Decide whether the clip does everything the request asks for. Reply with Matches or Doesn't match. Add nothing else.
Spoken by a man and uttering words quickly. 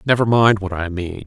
Matches